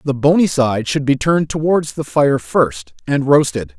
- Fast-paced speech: No, average, 190 wpm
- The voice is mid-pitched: No, low, 130 Hz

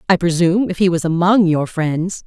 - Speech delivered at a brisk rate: Yes, fast, 210 wpm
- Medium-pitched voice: Yes, medium, 175 Hz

